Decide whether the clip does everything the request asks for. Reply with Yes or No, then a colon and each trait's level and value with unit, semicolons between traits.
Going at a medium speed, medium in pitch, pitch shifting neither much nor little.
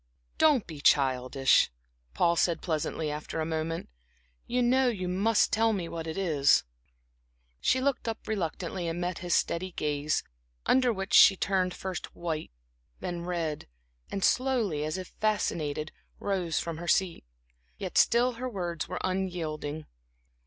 Yes: average, 145 wpm; medium, 175 Hz; average, 4.2 semitones